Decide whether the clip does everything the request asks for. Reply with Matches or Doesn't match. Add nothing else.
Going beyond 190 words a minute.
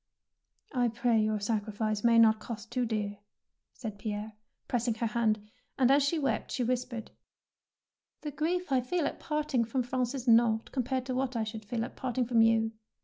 Matches